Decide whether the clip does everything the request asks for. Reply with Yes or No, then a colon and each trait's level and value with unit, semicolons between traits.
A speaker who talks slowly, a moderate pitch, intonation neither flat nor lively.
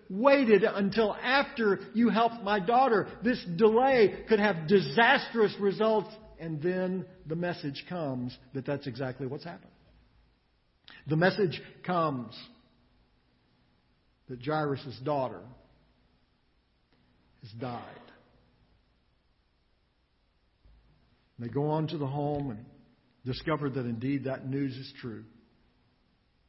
No: slow, 105 wpm; medium, 155 Hz; wide, 7.9 semitones